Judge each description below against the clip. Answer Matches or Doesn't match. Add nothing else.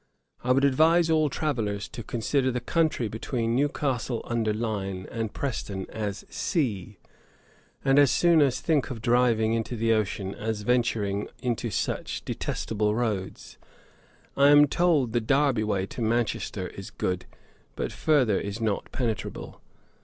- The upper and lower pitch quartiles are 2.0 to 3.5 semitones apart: Doesn't match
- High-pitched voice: Doesn't match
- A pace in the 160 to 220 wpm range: Doesn't match